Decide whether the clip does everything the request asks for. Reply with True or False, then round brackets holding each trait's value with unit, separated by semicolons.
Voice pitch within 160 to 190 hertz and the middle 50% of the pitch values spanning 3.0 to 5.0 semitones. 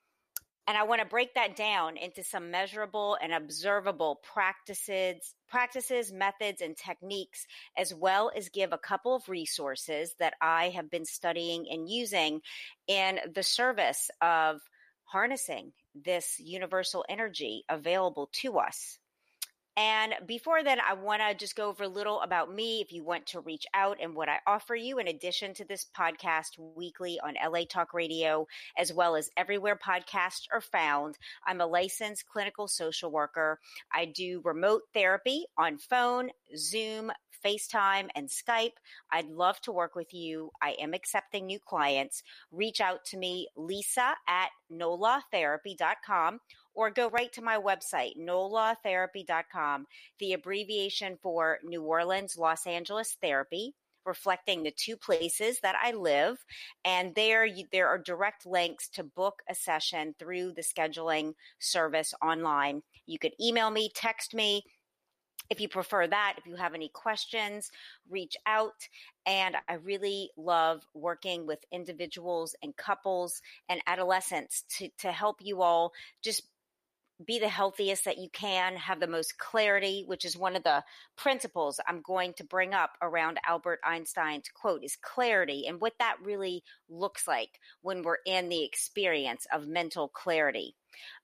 True (185 Hz; 3.7 semitones)